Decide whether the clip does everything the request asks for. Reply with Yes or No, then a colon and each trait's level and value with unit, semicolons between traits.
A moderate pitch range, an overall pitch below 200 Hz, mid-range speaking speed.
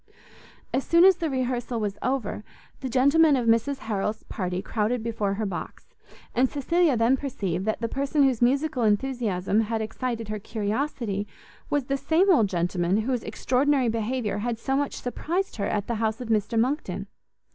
No: average, 4.2 semitones; high, 235 Hz; average, 170 wpm